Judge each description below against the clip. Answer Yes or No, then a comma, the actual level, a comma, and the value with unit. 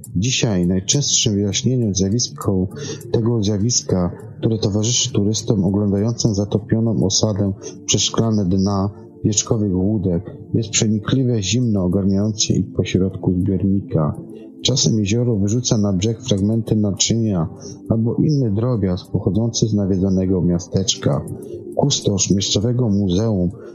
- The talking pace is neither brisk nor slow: No, slow, 100 wpm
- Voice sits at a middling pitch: No, low, 105 Hz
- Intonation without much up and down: No, average, 3.1 semitones